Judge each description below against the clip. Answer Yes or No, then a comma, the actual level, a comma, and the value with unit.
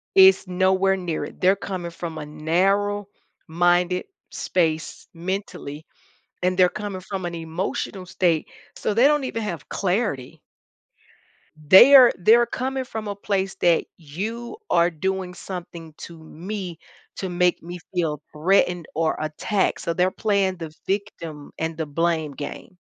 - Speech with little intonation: No, average, 3.2 semitones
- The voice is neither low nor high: Yes, medium, 180 Hz